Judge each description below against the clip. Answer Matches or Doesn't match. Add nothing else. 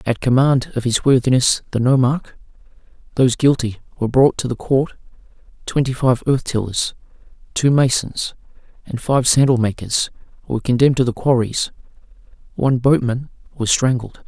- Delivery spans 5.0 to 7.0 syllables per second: Matches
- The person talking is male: Matches